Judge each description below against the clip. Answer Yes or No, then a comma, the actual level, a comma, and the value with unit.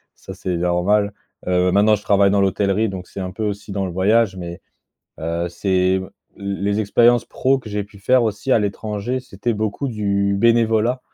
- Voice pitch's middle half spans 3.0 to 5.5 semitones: No, narrow, 2.6 semitones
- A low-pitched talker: Yes, low, 100 Hz